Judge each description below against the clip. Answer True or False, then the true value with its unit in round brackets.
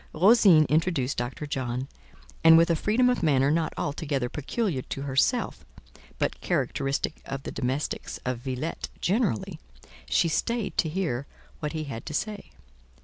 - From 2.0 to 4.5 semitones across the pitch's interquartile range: True (4.2 semitones)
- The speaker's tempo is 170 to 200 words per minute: False (145 wpm)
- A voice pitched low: False (150 Hz)